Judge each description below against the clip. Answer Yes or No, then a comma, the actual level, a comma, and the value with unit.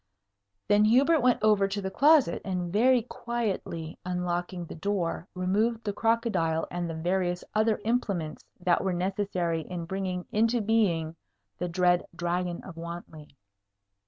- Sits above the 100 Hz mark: Yes, medium, 185 Hz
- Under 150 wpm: Yes, average, 140 wpm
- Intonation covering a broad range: No, average, 3.8 semitones